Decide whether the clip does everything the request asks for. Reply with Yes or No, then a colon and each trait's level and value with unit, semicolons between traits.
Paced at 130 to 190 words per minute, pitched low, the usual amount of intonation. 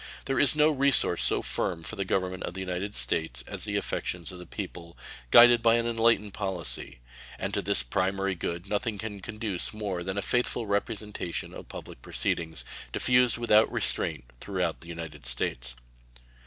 Yes: average, 170 wpm; very low, 95 Hz; average, 4.6 semitones